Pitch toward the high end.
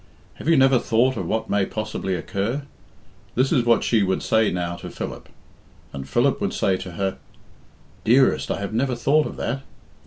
No: low, 110 Hz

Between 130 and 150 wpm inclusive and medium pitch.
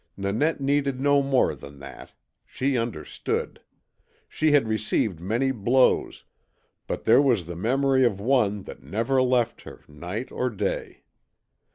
No: average, 140 wpm; low, 120 Hz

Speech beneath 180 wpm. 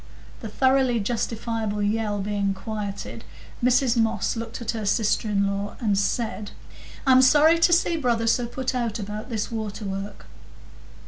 Yes: average, 150 wpm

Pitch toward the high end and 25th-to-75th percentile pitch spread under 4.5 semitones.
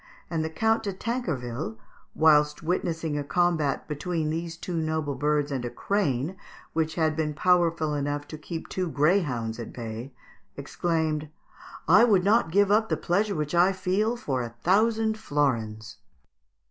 No: medium, 160 Hz; average, 4.1 semitones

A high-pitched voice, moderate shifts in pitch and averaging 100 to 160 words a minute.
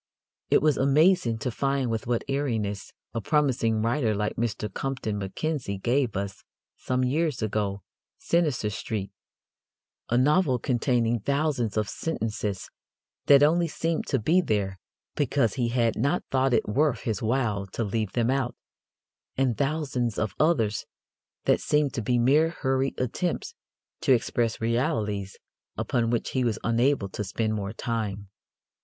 No: low, 120 Hz; average, 4.3 semitones; average, 145 wpm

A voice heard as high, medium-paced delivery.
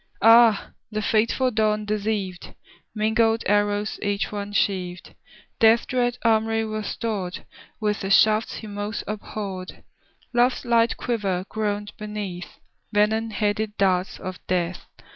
No: high, 210 Hz; slow, 125 wpm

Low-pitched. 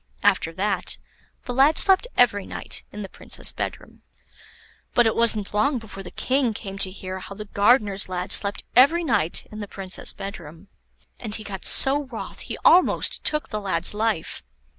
No: high, 210 Hz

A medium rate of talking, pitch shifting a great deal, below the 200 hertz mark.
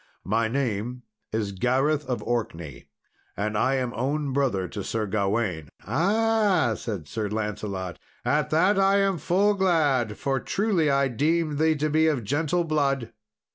Yes: average, 150 wpm; wide, 6.6 semitones; low, 135 Hz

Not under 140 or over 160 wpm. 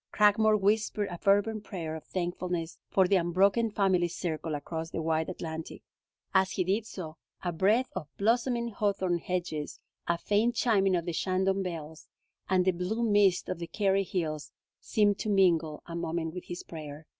No: average, 170 wpm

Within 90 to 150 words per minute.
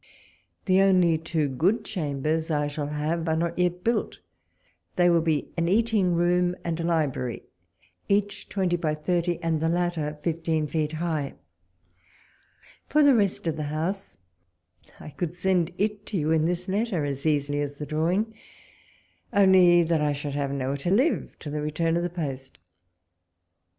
No: average, 165 wpm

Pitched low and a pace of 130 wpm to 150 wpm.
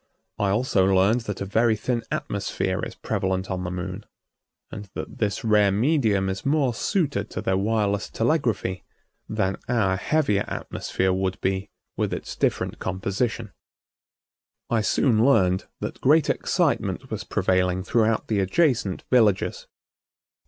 Yes: low, 100 Hz; average, 140 wpm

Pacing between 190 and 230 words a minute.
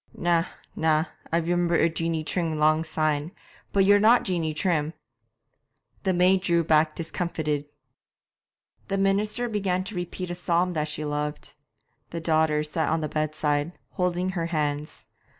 No: average, 150 wpm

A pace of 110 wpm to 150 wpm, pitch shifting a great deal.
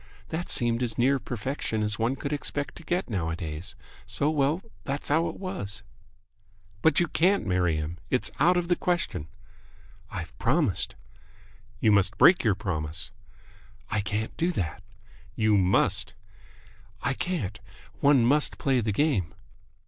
Yes: average, 145 wpm; wide, 7.5 semitones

